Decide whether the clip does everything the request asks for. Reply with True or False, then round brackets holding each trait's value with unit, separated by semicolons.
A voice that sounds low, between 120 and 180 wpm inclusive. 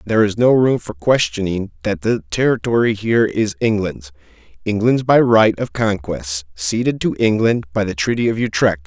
True (105 Hz; 160 wpm)